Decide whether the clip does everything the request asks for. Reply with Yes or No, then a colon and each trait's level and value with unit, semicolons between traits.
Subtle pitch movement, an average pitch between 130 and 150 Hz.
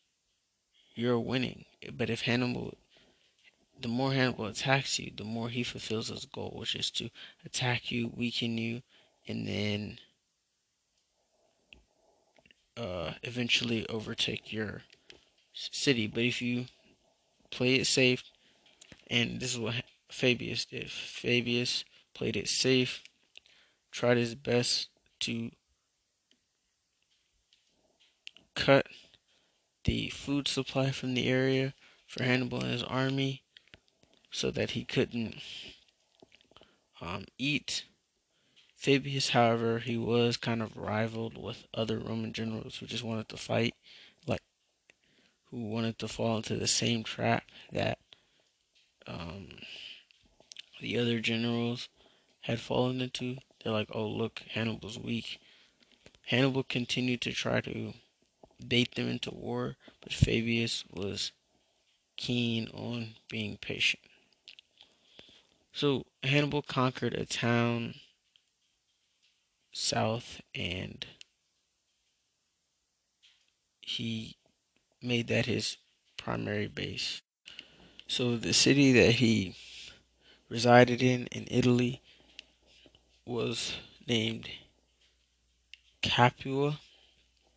No: narrow, 2.2 semitones; low, 120 Hz